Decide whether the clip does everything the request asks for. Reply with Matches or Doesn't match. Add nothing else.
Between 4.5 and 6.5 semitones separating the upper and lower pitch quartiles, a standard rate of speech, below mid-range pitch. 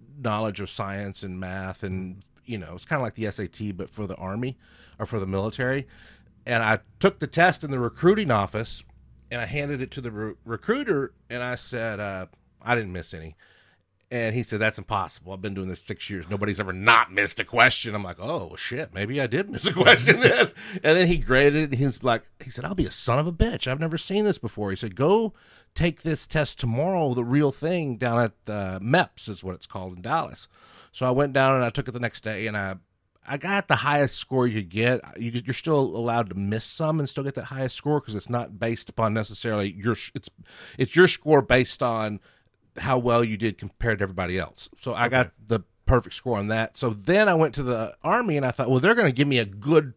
Doesn't match